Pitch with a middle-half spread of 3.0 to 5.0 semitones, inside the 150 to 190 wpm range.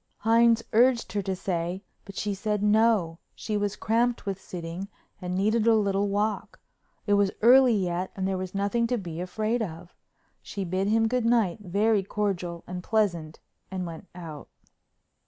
Yes: average, 3.5 semitones; average, 170 wpm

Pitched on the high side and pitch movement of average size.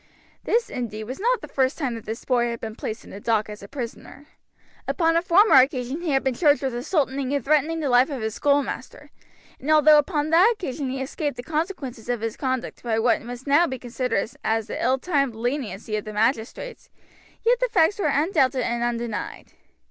Yes: very high, 265 Hz; average, 4.5 semitones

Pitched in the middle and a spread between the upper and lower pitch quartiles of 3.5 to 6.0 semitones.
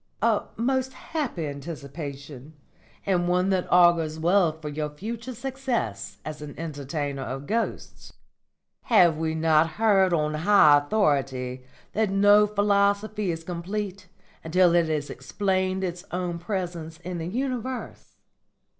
Yes: medium, 175 Hz; average, 5.0 semitones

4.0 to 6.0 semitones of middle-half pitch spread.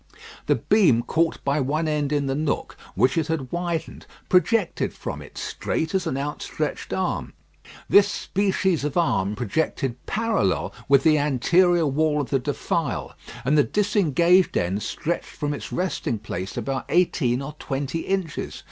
Yes: average, 4.4 semitones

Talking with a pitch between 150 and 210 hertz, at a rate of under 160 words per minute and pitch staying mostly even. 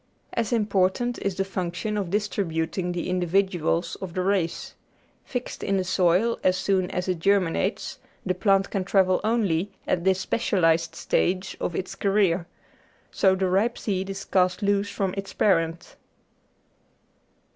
Yes: high, 190 Hz; average, 145 wpm; narrow, 1.9 semitones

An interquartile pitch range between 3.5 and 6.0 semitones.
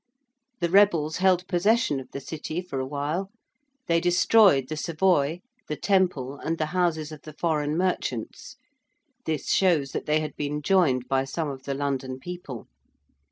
Yes: average, 4.2 semitones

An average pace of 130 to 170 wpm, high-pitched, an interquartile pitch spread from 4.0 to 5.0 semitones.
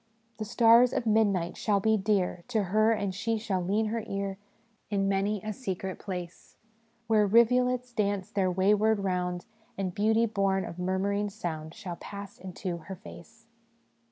No: average, 165 wpm; high, 200 Hz; average, 2.7 semitones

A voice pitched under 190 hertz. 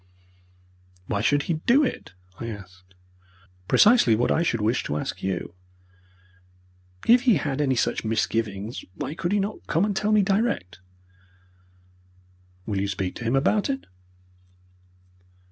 Yes: low, 135 Hz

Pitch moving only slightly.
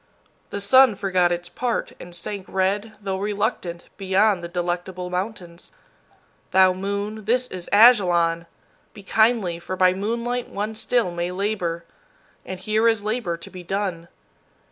No: average, 3.4 semitones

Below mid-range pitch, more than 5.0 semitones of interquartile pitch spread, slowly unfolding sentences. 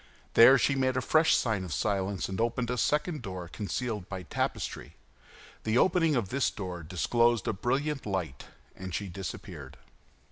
No: low, 110 Hz; wide, 5.6 semitones; average, 165 wpm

